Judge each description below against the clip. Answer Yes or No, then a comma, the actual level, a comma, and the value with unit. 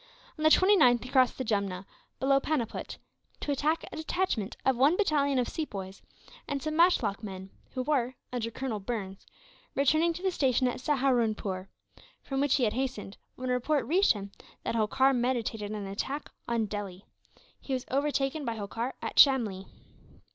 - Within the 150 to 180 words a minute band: Yes, average, 170 wpm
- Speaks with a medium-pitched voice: No, very high, 255 Hz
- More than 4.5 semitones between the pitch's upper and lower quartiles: Yes, average, 4.9 semitones